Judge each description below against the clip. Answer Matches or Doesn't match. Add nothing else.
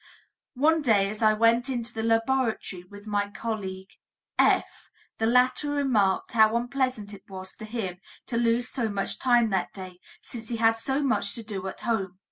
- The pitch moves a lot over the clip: Doesn't match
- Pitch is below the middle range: Doesn't match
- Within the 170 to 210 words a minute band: Matches